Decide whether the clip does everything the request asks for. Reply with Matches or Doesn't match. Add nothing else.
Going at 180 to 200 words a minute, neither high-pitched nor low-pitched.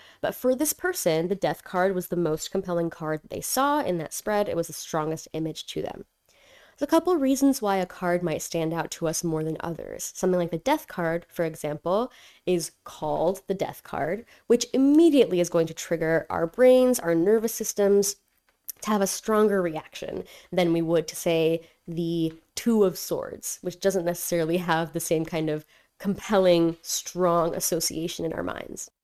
Matches